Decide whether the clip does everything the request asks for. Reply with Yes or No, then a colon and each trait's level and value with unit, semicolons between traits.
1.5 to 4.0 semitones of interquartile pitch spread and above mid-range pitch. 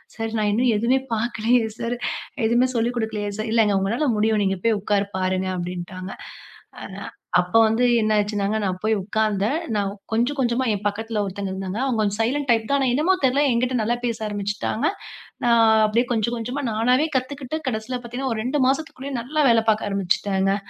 Yes: average, 3.2 semitones; high, 225 Hz